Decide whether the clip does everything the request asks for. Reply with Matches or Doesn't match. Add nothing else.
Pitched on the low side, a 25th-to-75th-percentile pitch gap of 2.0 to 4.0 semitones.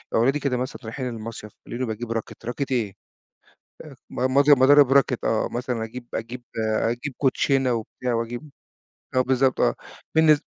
Matches